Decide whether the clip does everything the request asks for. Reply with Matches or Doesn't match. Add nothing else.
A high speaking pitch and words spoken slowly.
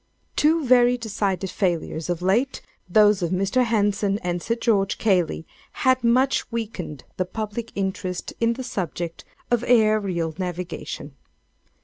Matches